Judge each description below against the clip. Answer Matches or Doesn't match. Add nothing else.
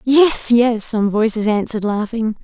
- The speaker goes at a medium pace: Matches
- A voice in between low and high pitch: Doesn't match